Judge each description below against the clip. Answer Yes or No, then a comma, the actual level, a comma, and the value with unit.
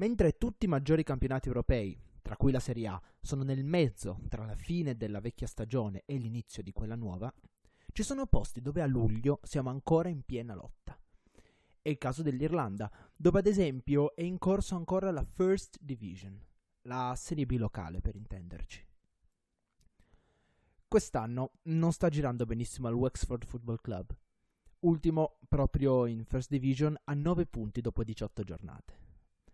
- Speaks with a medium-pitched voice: No, low, 130 Hz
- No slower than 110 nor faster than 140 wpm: No, average, 155 wpm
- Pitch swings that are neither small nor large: No, wide, 5.8 semitones